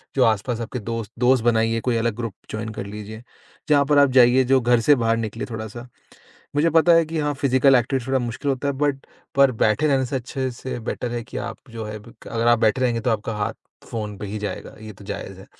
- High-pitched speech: No, low, 120 Hz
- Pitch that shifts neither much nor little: Yes, average, 3.1 semitones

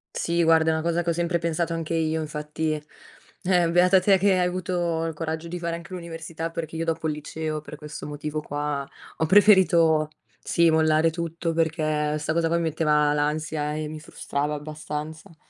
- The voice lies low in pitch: No, medium, 160 Hz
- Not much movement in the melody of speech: Yes, narrow, 1.7 semitones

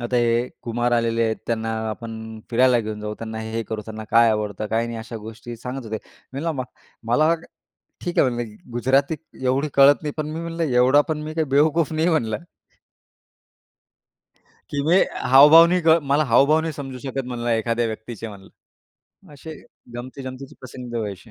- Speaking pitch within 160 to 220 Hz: No, low, 125 Hz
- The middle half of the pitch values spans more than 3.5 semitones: Yes, average, 4.3 semitones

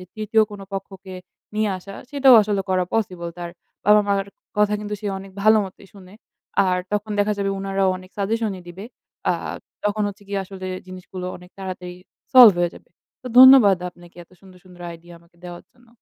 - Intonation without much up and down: Yes, narrow, 2.3 semitones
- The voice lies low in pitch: No, high, 195 Hz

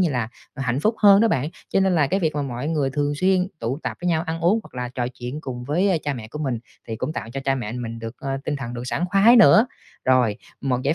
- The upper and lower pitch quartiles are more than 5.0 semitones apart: Yes, wide, 5.6 semitones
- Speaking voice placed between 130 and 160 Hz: Yes, medium, 140 Hz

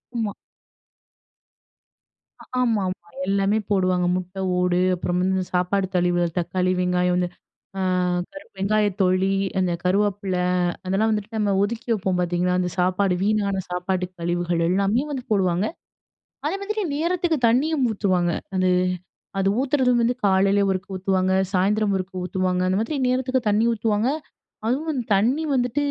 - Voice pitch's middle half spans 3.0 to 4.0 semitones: Yes, average, 3.6 semitones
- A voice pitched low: No, high, 195 Hz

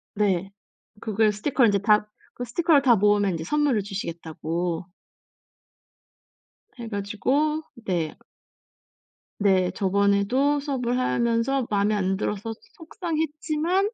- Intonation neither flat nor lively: No, wide, 5.8 semitones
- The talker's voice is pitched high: Yes, high, 215 Hz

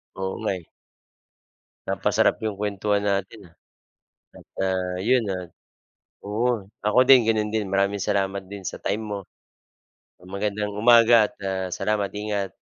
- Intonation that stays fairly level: Yes, narrow, 1.8 semitones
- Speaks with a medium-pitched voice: No, low, 100 Hz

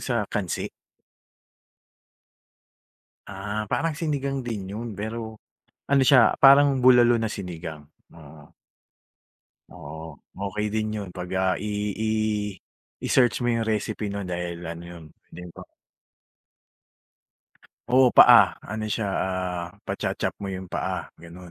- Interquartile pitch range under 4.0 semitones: No, average, 4.6 semitones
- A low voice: Yes, low, 105 Hz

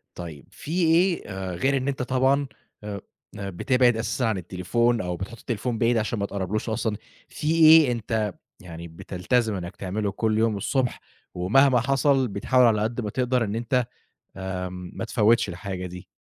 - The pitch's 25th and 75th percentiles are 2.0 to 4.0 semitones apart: No, average, 4.8 semitones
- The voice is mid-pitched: No, low, 110 Hz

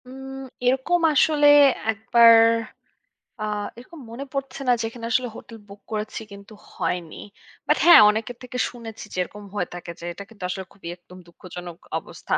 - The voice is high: Yes, high, 225 Hz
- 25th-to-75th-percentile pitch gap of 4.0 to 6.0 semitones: Yes, average, 4.3 semitones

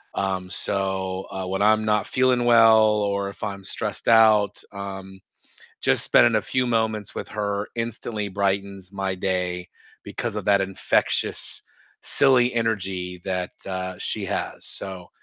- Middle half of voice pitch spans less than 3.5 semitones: Yes, narrow, 2.4 semitones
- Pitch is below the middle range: Yes, low, 100 Hz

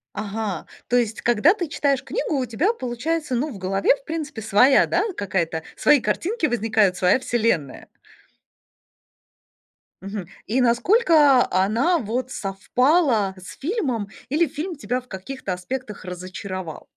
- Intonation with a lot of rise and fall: Yes, wide, 6.7 semitones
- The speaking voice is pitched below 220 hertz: No, high, 240 Hz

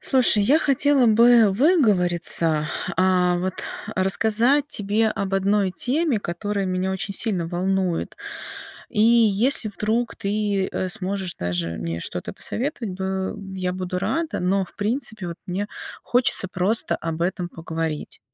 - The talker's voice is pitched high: Yes, high, 195 Hz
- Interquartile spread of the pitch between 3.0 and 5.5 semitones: Yes, average, 3.7 semitones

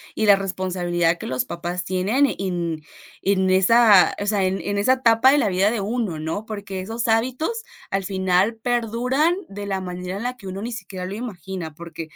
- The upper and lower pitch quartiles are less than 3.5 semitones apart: No, average, 3.8 semitones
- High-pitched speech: Yes, high, 195 Hz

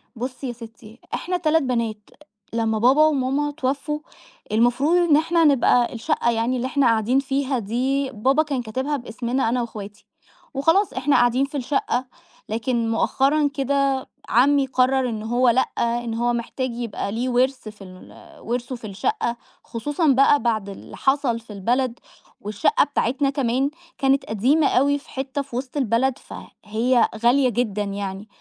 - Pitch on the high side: Yes, very high, 255 Hz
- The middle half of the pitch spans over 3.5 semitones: No, average, 3.2 semitones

